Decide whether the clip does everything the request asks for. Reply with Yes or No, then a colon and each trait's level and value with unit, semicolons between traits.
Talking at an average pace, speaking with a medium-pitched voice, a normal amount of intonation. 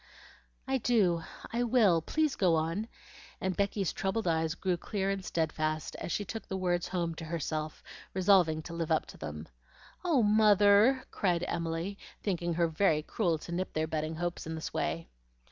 Yes: average, 175 wpm; medium, 175 Hz; average, 3.8 semitones